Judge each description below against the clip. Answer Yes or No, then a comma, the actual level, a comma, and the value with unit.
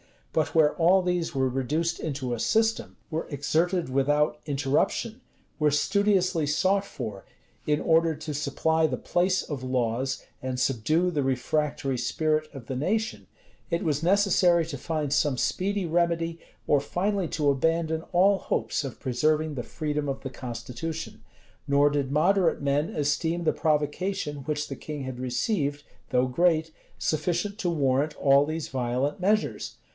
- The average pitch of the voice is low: No, medium, 150 Hz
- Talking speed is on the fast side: No, average, 150 wpm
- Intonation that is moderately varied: Yes, average, 3.8 semitones